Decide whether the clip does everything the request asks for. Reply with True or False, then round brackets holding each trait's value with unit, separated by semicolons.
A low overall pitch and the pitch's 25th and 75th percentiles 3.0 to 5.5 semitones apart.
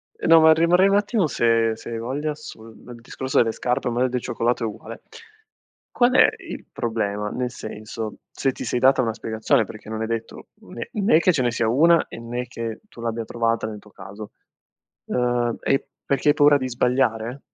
True (120 Hz; 3.4 semitones)